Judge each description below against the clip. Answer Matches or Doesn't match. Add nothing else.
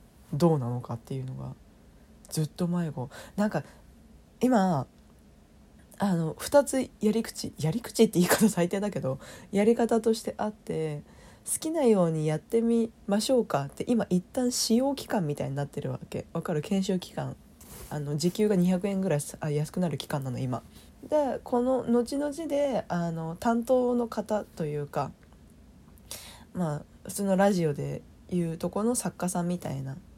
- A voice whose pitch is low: Doesn't match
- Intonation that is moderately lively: Doesn't match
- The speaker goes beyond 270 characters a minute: Matches